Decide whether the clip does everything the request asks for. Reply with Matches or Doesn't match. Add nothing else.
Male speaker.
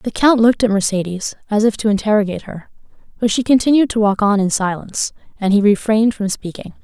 Doesn't match